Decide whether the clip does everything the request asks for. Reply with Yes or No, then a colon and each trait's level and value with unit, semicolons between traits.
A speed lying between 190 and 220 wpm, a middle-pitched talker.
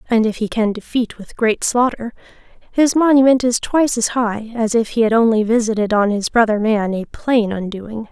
No: average, 200 wpm; high, 225 Hz